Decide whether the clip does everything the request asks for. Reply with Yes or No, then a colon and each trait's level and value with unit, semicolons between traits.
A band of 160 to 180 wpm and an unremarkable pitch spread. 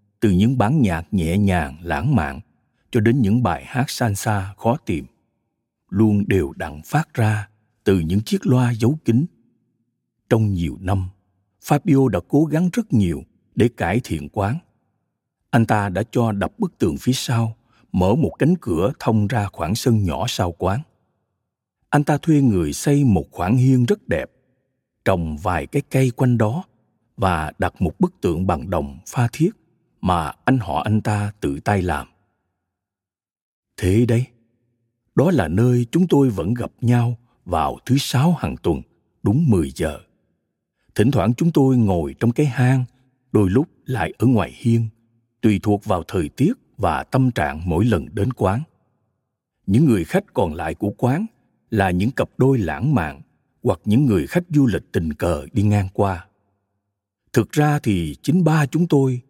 Yes: average, 170 wpm; average, 4.7 semitones